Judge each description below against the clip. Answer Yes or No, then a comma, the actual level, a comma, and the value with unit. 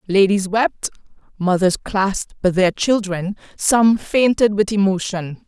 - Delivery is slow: Yes, slow, 110 wpm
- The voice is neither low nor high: No, high, 200 Hz